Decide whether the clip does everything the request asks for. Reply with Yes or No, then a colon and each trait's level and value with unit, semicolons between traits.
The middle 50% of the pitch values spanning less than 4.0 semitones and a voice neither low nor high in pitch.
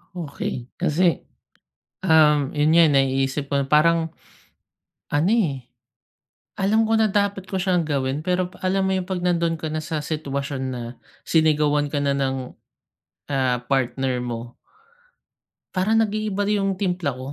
No: average, 5.2 semitones; medium, 155 Hz